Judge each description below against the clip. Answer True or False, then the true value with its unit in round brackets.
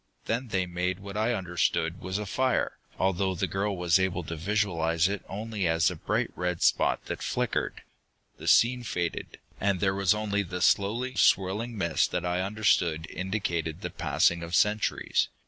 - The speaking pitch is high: False (95 Hz)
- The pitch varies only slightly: False (3.2 semitones)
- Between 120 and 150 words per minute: False (170 wpm)